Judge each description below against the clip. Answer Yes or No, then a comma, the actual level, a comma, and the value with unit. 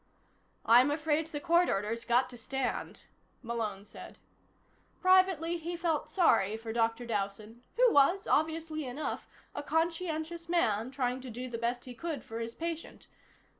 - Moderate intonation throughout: No, wide, 6.1 semitones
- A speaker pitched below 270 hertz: No, very high, 275 Hz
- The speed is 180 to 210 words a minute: No, average, 150 wpm